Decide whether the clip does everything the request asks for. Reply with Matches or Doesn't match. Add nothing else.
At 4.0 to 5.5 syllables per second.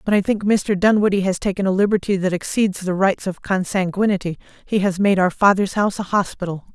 Doesn't match